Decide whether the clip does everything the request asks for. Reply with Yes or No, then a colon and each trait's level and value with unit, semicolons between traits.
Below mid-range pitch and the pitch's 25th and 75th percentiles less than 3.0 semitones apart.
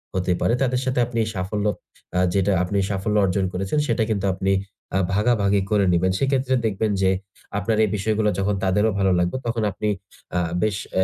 Yes: low, 105 Hz; narrow, 2.5 semitones